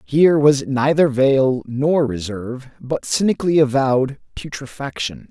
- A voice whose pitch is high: No, low, 135 Hz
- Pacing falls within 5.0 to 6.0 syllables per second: No, 4.5 syllables/s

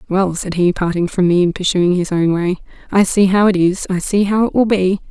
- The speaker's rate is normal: No, fast, 245 wpm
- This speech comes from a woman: Yes, female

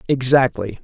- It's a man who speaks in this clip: Yes, male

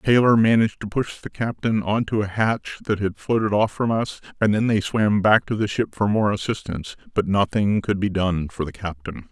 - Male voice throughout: Yes, male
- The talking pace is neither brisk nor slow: No, fast, 225 wpm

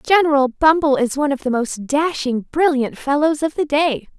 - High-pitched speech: Yes, very high, 285 Hz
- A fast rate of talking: No, average, 185 wpm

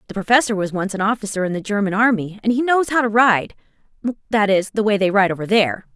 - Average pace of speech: No, fast, 230 wpm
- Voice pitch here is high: Yes, high, 210 Hz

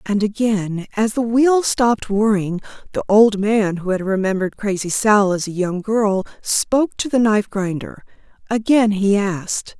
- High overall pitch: Yes, high, 210 Hz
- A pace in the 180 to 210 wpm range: No, average, 165 wpm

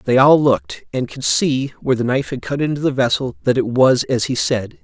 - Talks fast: Yes, fast, 250 wpm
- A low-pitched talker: Yes, low, 125 Hz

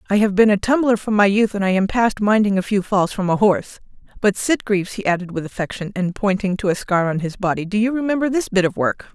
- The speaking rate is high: Yes, fast, 265 wpm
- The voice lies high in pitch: Yes, high, 205 Hz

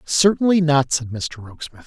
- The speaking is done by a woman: No, male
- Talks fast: No, average, 160 wpm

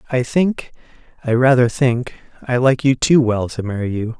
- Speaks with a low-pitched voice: Yes, low, 125 Hz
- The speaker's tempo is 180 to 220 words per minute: No, average, 170 wpm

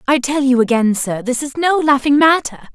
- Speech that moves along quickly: Yes, fast, 220 wpm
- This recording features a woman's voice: Yes, female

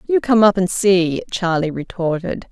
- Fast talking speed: No, average, 165 wpm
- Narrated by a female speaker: Yes, female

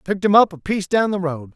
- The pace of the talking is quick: Yes, fast, 310 wpm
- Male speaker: Yes, male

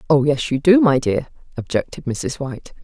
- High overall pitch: No, medium, 145 Hz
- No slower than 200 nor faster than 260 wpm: No, average, 190 wpm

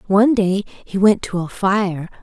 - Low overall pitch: No, high, 195 Hz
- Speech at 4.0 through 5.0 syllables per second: Yes, 4.2 syllables/s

